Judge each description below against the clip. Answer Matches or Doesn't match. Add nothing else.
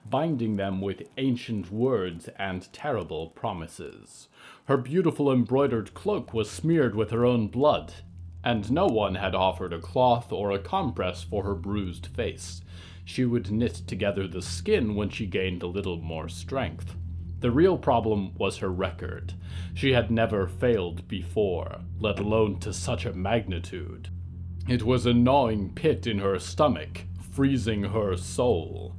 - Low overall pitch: Matches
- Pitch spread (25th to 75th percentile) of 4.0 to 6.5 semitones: Matches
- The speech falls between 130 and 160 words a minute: Matches